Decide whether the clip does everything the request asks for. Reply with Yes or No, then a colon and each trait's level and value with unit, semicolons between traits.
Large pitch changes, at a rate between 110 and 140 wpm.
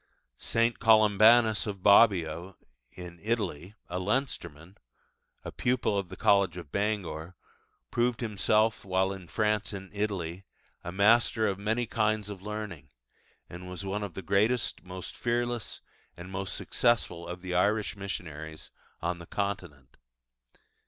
No: average, 3.3 semitones; slow, 135 wpm